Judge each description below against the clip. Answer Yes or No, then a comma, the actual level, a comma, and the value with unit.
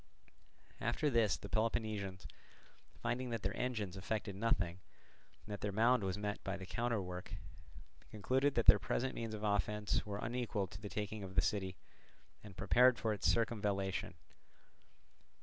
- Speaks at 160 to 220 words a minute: No, average, 150 wpm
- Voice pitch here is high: No, low, 105 Hz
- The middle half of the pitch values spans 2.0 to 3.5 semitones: Yes, average, 2.9 semitones